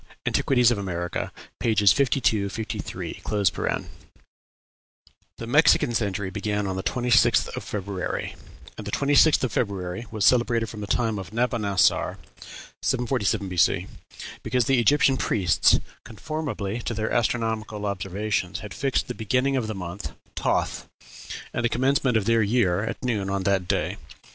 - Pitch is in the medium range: No, low, 110 Hz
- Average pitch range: Yes, average, 3.6 semitones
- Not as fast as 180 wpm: Yes, average, 140 wpm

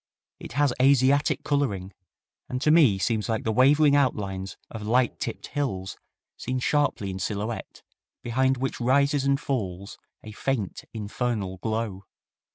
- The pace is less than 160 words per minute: Yes, average, 140 wpm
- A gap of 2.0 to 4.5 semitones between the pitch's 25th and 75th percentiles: No, average, 5.2 semitones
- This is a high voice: No, low, 120 Hz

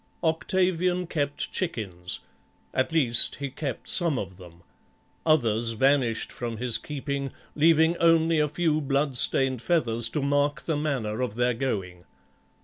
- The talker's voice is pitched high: No, medium, 140 Hz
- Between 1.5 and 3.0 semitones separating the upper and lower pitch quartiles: No, wide, 5.4 semitones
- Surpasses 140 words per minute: No, slow, 135 wpm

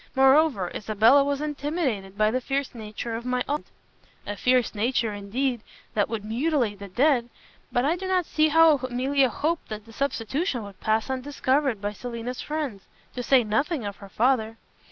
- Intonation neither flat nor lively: Yes, average, 4.6 semitones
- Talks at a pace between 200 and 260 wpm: No, average, 175 wpm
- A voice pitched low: No, very high, 250 Hz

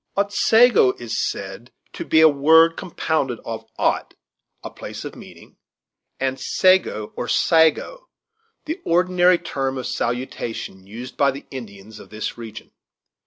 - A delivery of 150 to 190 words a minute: No, slow, 135 wpm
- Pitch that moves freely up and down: Yes, wide, 7.0 semitones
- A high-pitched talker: No, low, 135 Hz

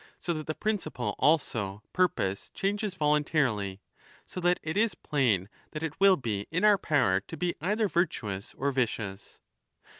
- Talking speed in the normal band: Yes, average, 155 wpm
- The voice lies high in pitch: No, medium, 150 Hz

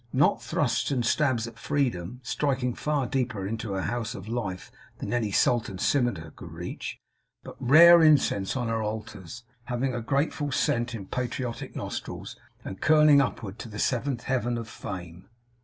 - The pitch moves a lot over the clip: No, average, 3.9 semitones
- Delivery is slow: No, average, 160 wpm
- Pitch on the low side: Yes, low, 120 Hz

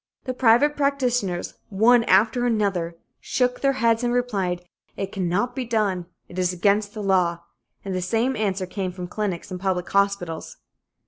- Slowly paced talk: No, average, 165 wpm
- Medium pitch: No, high, 200 Hz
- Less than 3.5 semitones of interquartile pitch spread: No, average, 4.7 semitones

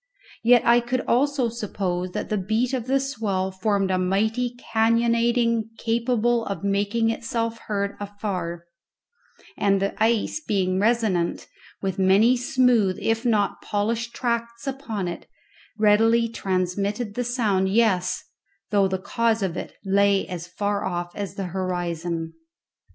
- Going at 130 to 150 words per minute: Yes, slow, 135 wpm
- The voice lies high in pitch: Yes, high, 210 Hz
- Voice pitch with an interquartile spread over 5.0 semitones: No, average, 3.5 semitones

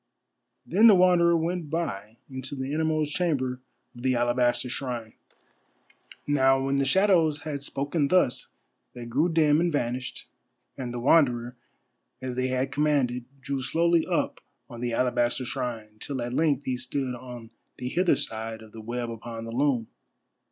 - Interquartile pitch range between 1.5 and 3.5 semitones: No, average, 3.9 semitones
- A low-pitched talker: Yes, low, 130 Hz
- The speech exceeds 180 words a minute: No, average, 160 wpm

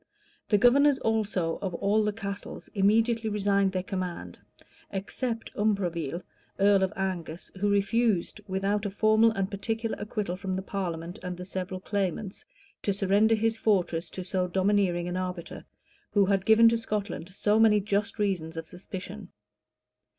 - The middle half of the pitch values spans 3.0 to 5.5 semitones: No, narrow, 2.5 semitones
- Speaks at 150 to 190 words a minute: Yes, average, 155 wpm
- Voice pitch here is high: Yes, high, 200 Hz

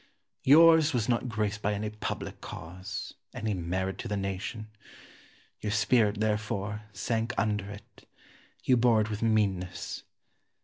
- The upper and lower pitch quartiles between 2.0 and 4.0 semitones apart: Yes, narrow, 2.5 semitones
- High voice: No, low, 105 Hz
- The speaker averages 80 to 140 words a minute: Yes, slow, 135 wpm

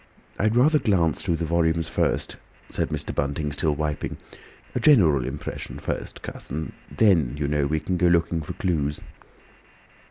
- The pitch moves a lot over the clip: No, average, 3.3 semitones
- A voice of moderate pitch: No, very low, 80 Hz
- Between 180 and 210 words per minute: No, average, 160 wpm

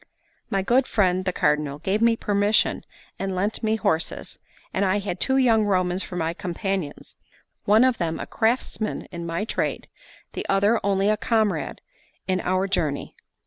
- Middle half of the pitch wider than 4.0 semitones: No, average, 3.3 semitones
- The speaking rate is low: No, average, 165 wpm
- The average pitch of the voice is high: Yes, high, 195 Hz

